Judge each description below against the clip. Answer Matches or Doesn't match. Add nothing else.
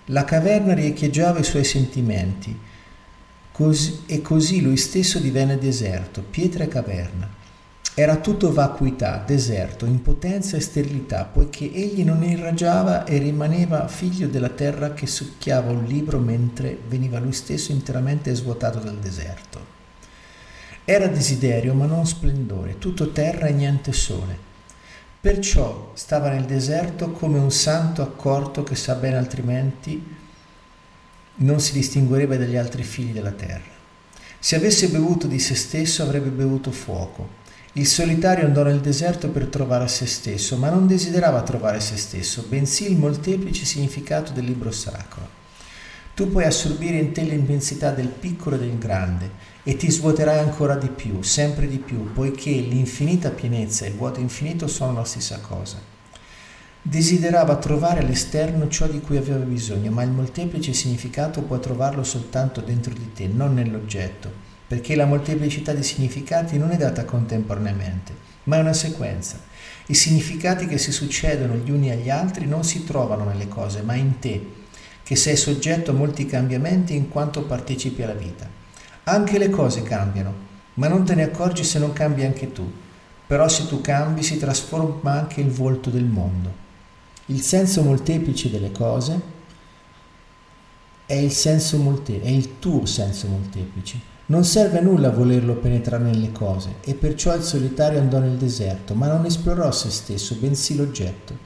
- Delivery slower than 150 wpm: Doesn't match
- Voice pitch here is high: Doesn't match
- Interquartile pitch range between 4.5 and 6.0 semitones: Matches